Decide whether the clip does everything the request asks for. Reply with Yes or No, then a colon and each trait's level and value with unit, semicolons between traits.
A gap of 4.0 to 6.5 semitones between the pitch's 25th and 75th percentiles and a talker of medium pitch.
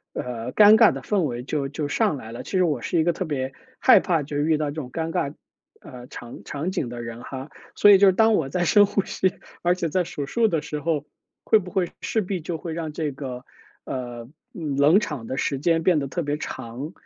Yes: average, 4.9 semitones; medium, 150 Hz